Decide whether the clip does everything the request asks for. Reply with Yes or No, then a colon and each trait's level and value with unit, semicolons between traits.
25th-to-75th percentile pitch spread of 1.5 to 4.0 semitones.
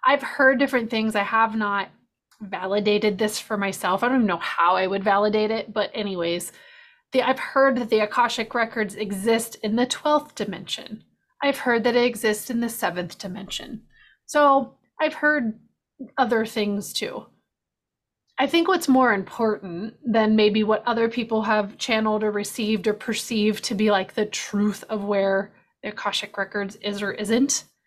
Yes: average, 2.9 semitones